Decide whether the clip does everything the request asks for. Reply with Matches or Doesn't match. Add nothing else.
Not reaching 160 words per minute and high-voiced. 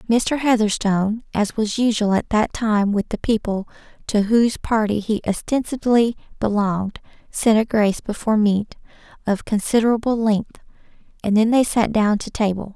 Matches